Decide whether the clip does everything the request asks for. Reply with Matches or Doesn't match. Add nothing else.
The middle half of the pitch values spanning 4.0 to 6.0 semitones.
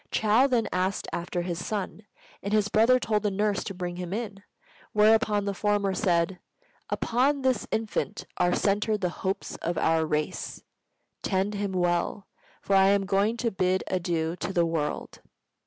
Doesn't match